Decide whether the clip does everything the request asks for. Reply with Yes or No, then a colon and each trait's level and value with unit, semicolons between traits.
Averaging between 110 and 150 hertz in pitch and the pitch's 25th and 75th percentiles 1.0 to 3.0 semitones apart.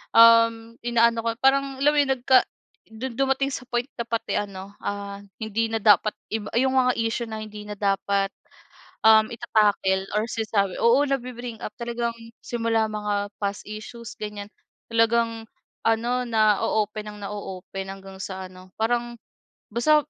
No: high, 225 Hz; narrow, 2.4 semitones